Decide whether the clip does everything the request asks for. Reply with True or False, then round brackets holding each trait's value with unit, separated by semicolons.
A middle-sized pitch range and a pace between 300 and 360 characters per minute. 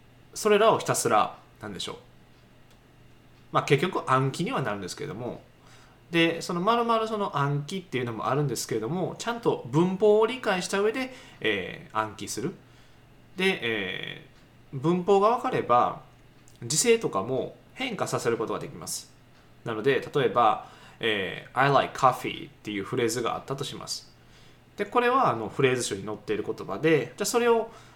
False (9.0 semitones; 350 characters per minute)